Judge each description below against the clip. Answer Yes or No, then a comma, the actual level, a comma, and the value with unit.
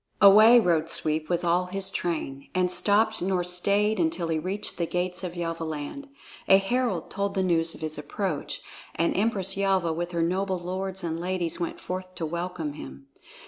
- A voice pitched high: No, medium, 180 Hz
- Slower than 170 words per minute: No, average, 180 wpm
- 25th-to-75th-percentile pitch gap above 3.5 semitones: No, average, 2.7 semitones